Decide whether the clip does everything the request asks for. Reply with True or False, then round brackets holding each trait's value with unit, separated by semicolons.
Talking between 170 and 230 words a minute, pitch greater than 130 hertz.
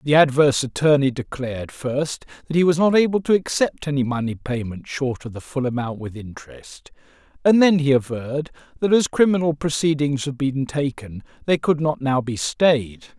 True (175 wpm; 140 Hz)